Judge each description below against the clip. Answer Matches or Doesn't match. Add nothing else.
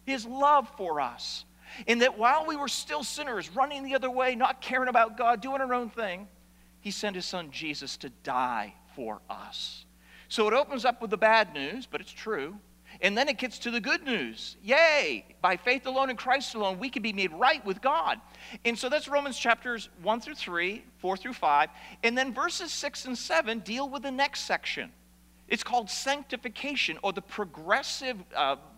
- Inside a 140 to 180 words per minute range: Doesn't match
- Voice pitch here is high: Matches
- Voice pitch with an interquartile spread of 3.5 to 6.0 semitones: Matches